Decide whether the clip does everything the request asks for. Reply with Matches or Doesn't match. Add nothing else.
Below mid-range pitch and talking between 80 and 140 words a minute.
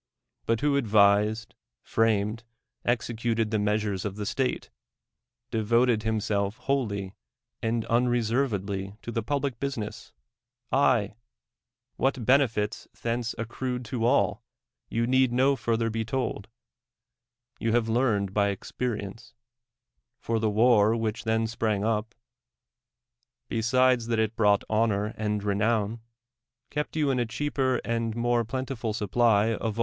Matches